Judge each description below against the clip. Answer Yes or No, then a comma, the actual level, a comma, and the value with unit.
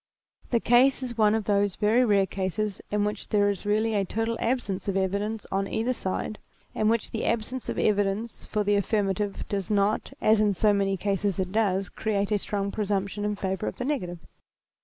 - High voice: Yes, high, 205 Hz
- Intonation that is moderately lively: No, narrow, 1.8 semitones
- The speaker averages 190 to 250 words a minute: Yes, average, 195 wpm